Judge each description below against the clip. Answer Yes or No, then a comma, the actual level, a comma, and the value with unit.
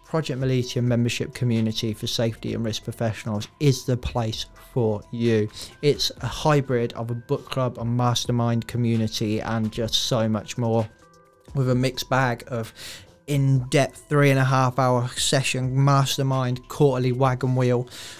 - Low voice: Yes, low, 120 Hz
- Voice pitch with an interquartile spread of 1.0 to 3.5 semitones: Yes, narrow, 2.6 semitones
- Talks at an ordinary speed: Yes, average, 150 wpm